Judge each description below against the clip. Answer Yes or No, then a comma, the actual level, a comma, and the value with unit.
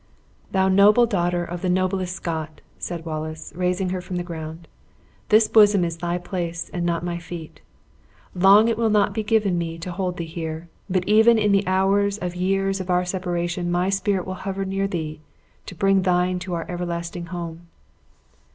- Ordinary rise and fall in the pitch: No, narrow, 2.2 semitones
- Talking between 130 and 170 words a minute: No, average, 185 wpm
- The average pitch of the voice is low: No, medium, 180 Hz